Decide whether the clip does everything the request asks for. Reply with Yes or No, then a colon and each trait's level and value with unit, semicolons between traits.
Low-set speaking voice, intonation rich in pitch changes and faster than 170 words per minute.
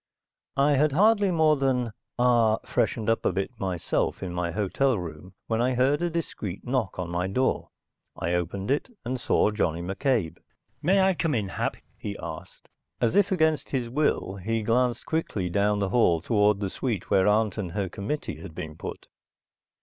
Yes: low, 110 Hz; wide, 6.2 semitones; average, 180 wpm